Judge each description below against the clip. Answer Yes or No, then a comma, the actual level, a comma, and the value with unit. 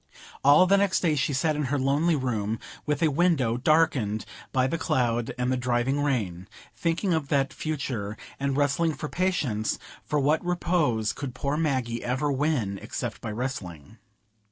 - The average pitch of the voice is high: No, low, 135 Hz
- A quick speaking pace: No, average, 165 wpm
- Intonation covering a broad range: No, average, 4.4 semitones